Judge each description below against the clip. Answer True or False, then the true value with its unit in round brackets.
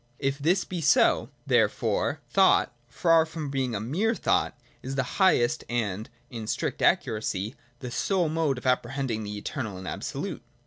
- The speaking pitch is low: True (130 Hz)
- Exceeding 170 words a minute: False (165 wpm)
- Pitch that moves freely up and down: True (6.1 semitones)